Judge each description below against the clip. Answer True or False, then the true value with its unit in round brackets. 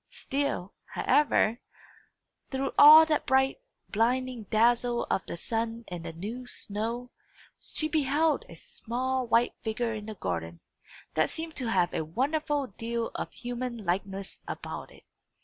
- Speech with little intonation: False (4.3 semitones)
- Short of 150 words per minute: True (140 wpm)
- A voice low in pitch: False (235 Hz)